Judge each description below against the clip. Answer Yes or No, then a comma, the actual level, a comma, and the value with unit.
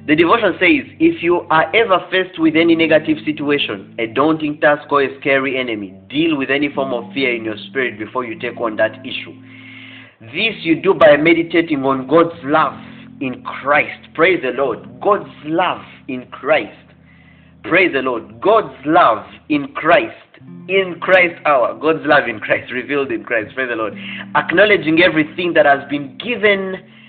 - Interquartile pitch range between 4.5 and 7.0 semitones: Yes, average, 5.3 semitones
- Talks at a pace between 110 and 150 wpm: No, average, 170 wpm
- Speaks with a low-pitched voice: No, medium, 150 Hz